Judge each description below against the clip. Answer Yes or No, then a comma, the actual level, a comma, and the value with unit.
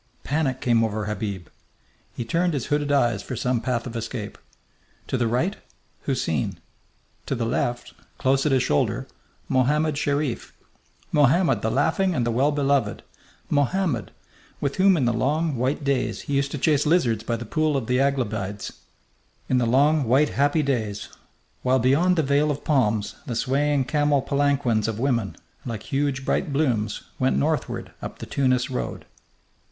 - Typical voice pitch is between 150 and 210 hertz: No, low, 130 Hz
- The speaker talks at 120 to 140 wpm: No, average, 165 wpm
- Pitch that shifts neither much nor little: Yes, average, 3.8 semitones